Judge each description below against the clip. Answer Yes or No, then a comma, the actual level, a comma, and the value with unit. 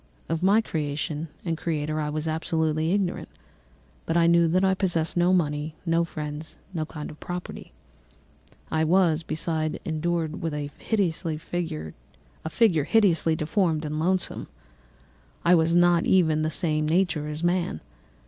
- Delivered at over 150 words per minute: No, average, 145 wpm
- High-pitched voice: No, medium, 160 Hz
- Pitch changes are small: Yes, narrow, 2.2 semitones